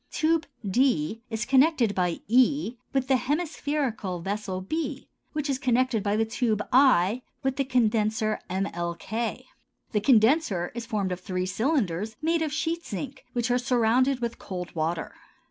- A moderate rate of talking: Yes, average, 150 wpm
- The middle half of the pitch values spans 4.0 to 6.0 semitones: Yes, average, 5.1 semitones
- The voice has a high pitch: Yes, high, 235 Hz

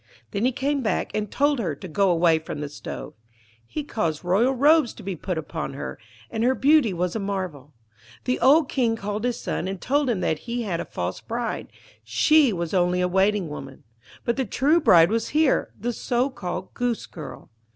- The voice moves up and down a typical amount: No, wide, 6.5 semitones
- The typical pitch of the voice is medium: No, high, 210 Hz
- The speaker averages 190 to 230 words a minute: Yes, average, 200 wpm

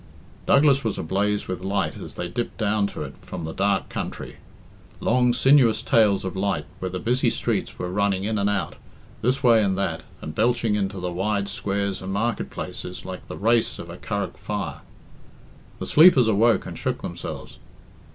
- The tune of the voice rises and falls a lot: No, average, 3.3 semitones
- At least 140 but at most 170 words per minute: No, average, 180 wpm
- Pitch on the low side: Yes, low, 100 Hz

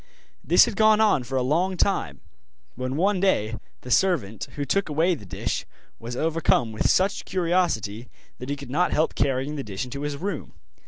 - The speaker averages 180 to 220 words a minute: Yes, average, 190 wpm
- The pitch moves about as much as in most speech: No, wide, 6.7 semitones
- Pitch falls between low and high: Yes, medium, 145 Hz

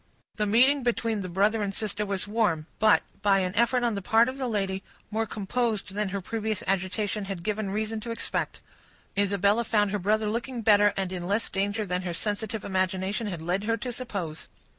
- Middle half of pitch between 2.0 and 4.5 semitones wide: Yes, narrow, 2.4 semitones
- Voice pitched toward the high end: Yes, high, 205 Hz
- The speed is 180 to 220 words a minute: Yes, average, 200 wpm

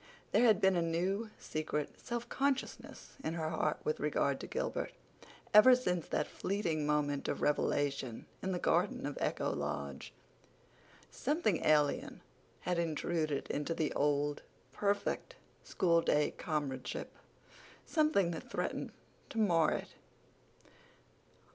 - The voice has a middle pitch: Yes, medium, 165 Hz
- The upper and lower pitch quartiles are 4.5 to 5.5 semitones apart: Yes, average, 5.0 semitones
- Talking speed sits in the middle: No, slow, 125 wpm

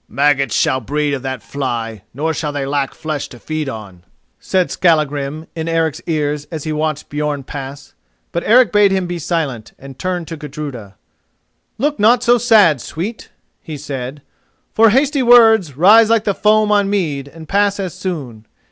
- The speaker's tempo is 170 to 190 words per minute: Yes, average, 175 wpm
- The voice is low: No, medium, 155 Hz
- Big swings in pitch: Yes, wide, 6.1 semitones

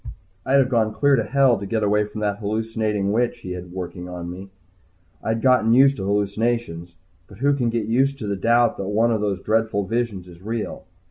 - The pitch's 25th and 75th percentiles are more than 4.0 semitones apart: No, average, 3.1 semitones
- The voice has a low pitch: Yes, low, 110 Hz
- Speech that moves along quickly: Yes, fast, 210 wpm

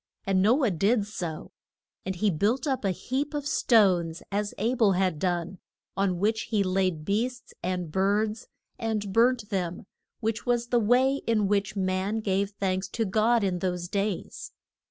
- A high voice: Yes, high, 200 Hz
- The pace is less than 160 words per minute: No, average, 170 wpm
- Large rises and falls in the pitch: No, average, 3.4 semitones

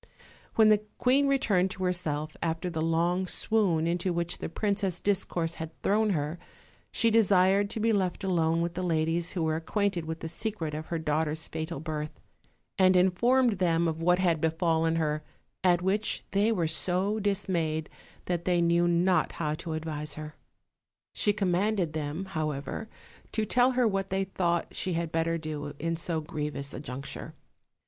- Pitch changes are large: No, average, 3.3 semitones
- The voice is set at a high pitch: No, medium, 170 Hz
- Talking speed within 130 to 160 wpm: No, average, 170 wpm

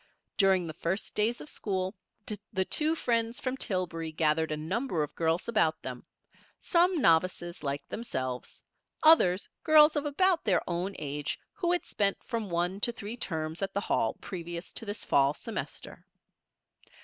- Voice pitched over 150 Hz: Yes, high, 190 Hz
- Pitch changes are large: Yes, wide, 6.3 semitones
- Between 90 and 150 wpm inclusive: No, average, 160 wpm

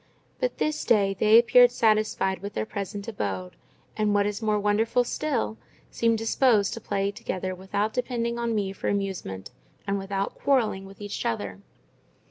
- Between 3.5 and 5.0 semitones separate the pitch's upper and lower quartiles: No, average, 3.0 semitones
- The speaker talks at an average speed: Yes, average, 160 wpm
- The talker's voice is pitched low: No, high, 205 Hz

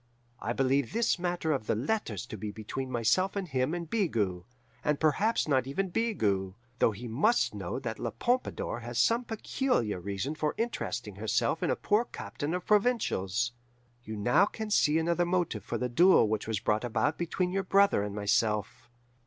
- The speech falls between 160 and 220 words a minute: Yes, average, 180 wpm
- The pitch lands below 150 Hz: Yes, low, 135 Hz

